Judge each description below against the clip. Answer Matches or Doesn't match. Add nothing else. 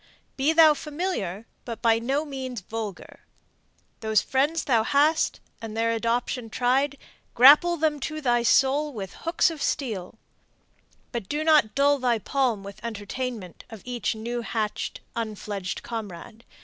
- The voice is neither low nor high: Doesn't match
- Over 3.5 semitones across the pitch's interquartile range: Matches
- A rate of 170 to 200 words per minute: Doesn't match